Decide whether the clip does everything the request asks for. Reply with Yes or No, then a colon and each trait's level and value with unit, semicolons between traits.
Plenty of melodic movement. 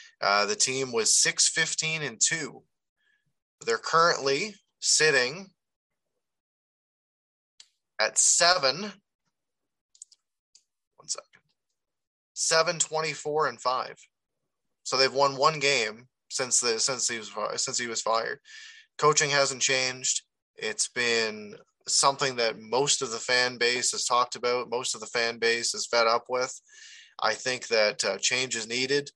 Yes: wide, 7.6 semitones